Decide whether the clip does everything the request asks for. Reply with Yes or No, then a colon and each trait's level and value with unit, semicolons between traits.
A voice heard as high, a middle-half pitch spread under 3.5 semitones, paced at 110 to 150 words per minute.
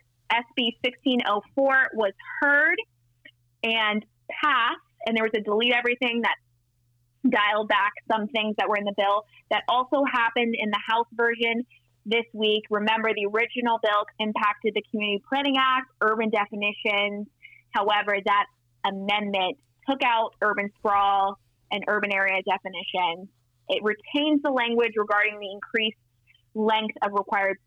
Yes: high, 210 Hz; average, 2.7 semitones; slow, 135 wpm